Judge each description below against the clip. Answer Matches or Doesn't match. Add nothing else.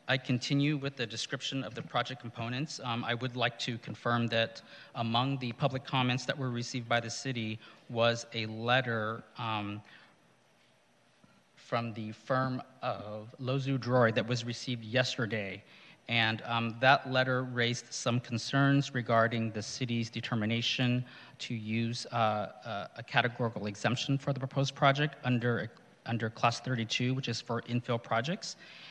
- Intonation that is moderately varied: Doesn't match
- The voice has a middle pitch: Doesn't match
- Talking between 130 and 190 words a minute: Matches